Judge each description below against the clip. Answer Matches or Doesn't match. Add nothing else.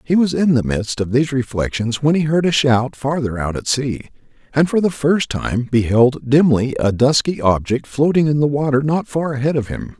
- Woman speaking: Doesn't match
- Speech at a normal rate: Doesn't match